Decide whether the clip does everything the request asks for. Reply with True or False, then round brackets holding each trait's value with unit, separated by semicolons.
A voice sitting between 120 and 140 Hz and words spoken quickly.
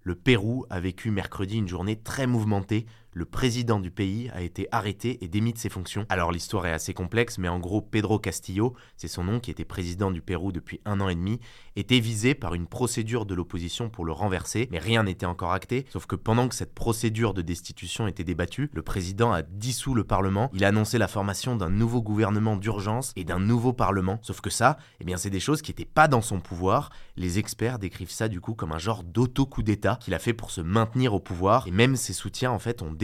False (105 Hz; 230 wpm)